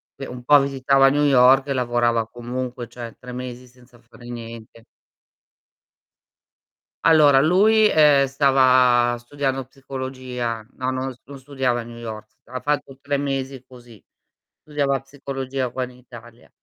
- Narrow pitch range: Yes, narrow, 2.2 semitones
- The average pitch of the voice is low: Yes, low, 130 Hz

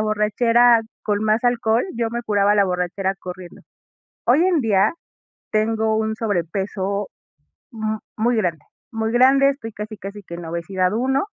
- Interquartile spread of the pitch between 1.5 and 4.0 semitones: Yes, average, 2.9 semitones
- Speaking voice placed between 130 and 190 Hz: No, high, 215 Hz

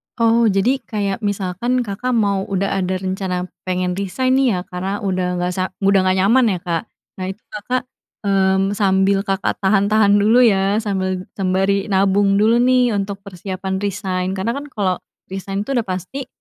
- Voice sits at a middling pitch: No, high, 195 Hz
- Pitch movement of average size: No, narrow, 2.2 semitones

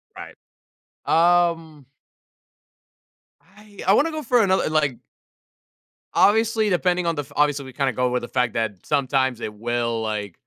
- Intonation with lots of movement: Yes, wide, 6.9 semitones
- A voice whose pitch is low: No, medium, 145 Hz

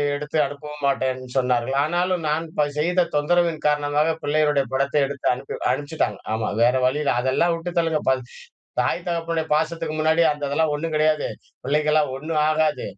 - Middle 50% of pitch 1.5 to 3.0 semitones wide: Yes, narrow, 2.5 semitones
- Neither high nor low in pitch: Yes, medium, 150 Hz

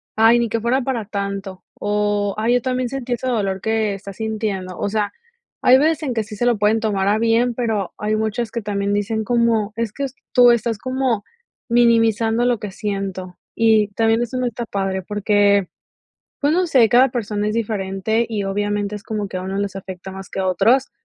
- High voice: Yes, high, 220 Hz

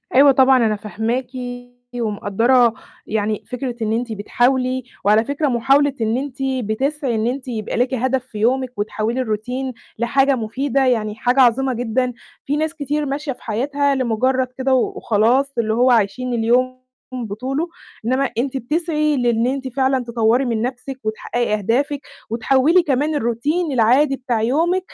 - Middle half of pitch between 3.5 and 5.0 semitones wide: No, average, 3.0 semitones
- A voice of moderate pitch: No, very high, 255 Hz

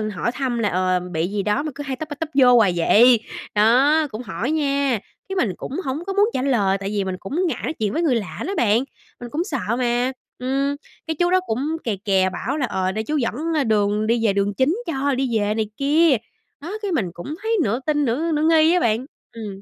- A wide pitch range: Yes, wide, 6.2 semitones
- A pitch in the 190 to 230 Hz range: No, very high, 250 Hz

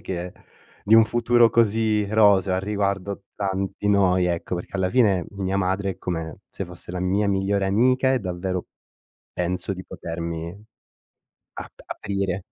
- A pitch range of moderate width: No, narrow, 2.0 semitones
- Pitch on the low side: Yes, very low, 95 Hz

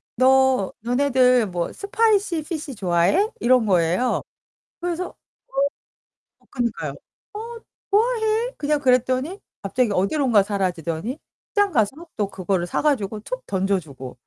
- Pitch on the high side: Yes, very high, 250 Hz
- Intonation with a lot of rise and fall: Yes, wide, 8.9 semitones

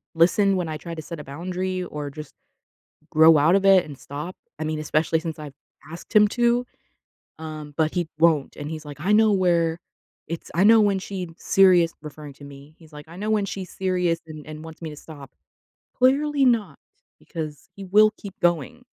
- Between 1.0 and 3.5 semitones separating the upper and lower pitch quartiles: No, average, 3.9 semitones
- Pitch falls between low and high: Yes, medium, 165 Hz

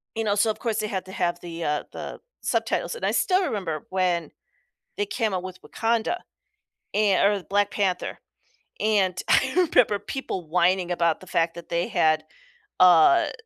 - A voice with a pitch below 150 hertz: No, high, 190 Hz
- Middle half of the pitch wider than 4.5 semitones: No, average, 4.2 semitones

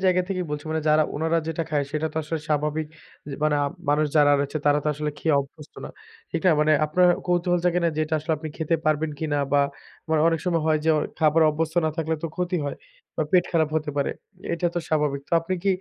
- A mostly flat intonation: Yes, narrow, 1.8 semitones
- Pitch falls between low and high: Yes, medium, 155 Hz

